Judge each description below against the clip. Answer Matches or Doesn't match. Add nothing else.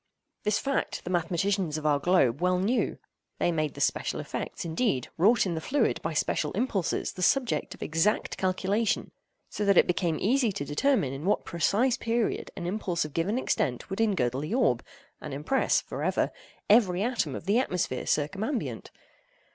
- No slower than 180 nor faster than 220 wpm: Doesn't match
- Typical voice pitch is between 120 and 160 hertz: Doesn't match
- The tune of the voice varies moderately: Doesn't match